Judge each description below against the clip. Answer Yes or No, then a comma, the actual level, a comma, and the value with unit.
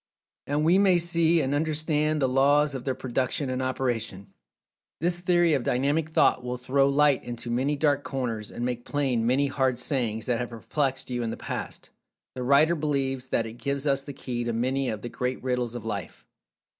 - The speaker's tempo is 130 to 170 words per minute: No, average, 195 wpm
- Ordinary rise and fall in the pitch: Yes, average, 3.1 semitones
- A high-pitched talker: No, low, 135 Hz